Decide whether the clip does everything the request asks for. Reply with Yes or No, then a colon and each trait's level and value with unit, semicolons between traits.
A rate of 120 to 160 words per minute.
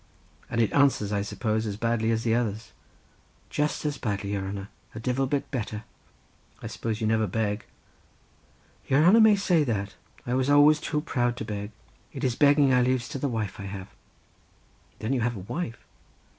No: average, 185 wpm